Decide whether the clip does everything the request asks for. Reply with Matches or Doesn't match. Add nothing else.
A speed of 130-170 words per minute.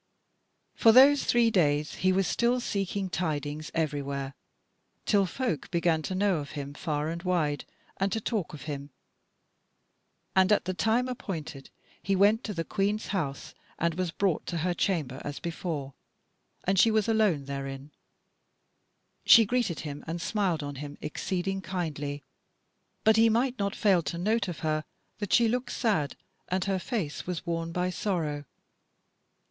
Matches